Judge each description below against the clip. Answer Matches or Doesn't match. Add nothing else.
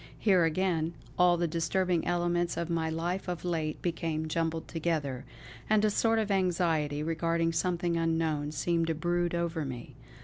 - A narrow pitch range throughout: Matches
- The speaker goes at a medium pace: Matches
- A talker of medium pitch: Matches